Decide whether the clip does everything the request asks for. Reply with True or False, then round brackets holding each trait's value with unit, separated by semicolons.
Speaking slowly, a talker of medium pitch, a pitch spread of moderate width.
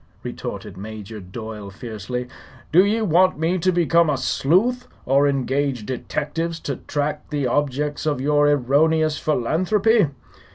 True (130 wpm; 145 Hz; 4.9 semitones)